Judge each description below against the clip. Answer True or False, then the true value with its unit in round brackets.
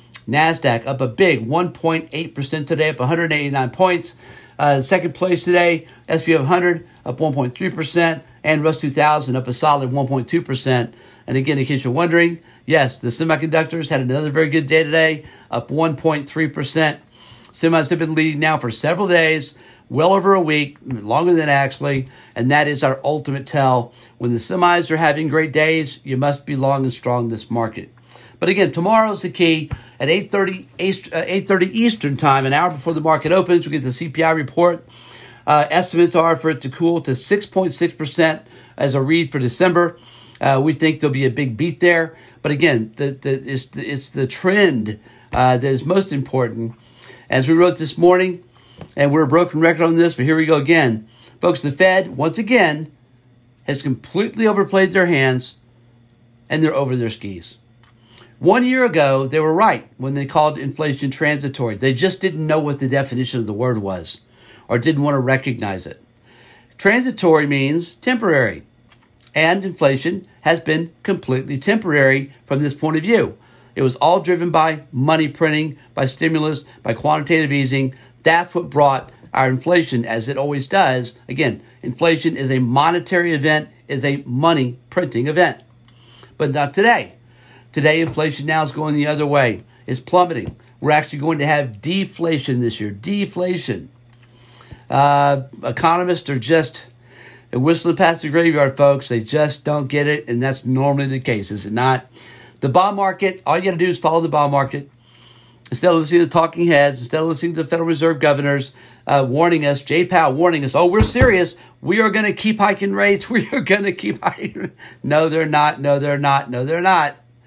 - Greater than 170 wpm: True (185 wpm)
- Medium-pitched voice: True (145 Hz)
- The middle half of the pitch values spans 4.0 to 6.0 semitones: True (4.7 semitones)